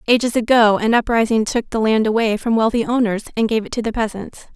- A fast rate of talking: Yes, fast, 225 wpm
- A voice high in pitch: Yes, high, 225 Hz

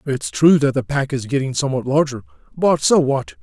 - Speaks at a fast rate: Yes, fast, 210 wpm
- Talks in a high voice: No, low, 135 Hz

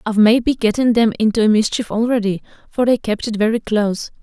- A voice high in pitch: Yes, high, 220 Hz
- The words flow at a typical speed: Yes, average, 185 wpm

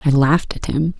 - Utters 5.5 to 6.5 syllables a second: Yes, 5.7 syllables/s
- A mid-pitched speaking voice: Yes, medium, 150 Hz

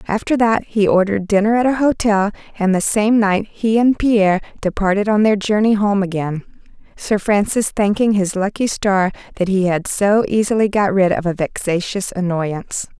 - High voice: Yes, high, 205 Hz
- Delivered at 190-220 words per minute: No, average, 175 wpm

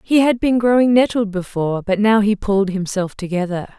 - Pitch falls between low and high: No, high, 205 Hz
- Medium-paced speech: Yes, average, 190 wpm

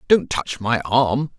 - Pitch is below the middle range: Yes, low, 125 Hz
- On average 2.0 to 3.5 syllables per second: Yes, 3.4 syllables/s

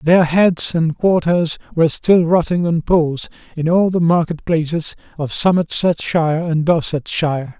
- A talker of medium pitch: Yes, medium, 165 Hz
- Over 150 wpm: No, average, 140 wpm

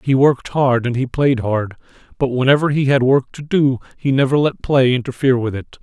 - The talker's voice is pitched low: Yes, low, 130 Hz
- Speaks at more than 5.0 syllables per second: Yes, 5.5 syllables/s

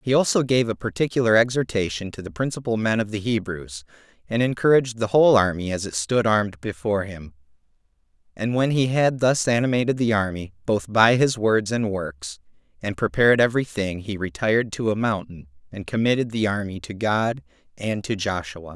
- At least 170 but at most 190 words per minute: Yes, average, 180 wpm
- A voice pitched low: Yes, low, 110 Hz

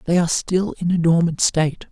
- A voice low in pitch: No, medium, 170 Hz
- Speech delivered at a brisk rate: Yes, fast, 220 wpm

